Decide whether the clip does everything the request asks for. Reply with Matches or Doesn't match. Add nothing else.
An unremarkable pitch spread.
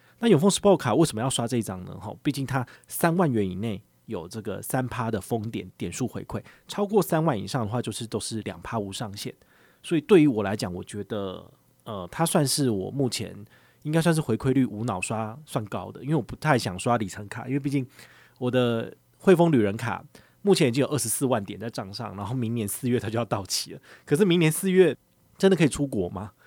Matches